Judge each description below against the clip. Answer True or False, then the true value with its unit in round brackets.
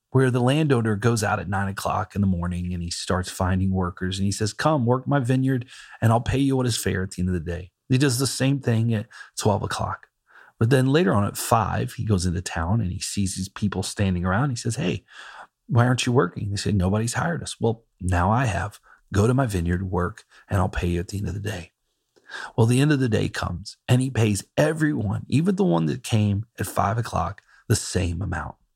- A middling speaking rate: False (240 wpm)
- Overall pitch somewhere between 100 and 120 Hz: True (105 Hz)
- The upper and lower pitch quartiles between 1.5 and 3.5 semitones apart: False (5.2 semitones)